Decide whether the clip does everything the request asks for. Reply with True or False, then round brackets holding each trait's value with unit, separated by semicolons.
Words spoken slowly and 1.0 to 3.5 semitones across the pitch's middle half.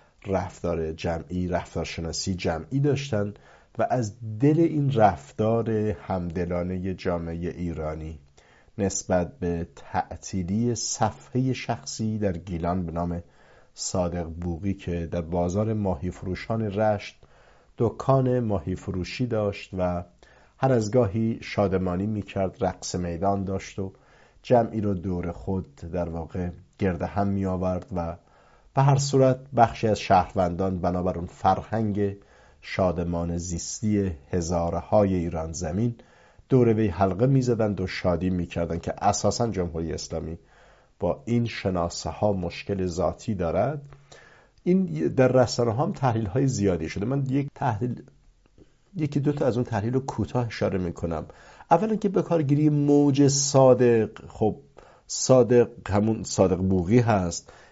False (125 wpm; 5.2 semitones)